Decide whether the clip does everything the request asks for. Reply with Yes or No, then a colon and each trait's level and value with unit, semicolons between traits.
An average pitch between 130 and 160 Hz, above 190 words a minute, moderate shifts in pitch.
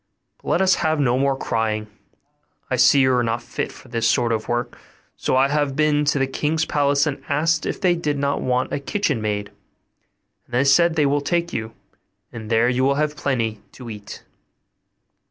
Yes: low, 135 Hz; average, 200 wpm; average, 4.0 semitones